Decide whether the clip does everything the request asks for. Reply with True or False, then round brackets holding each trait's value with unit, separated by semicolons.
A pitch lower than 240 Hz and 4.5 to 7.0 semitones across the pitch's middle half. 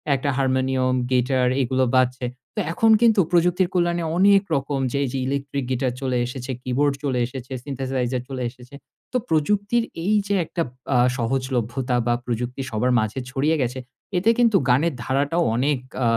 False (135 Hz; 3.9 semitones)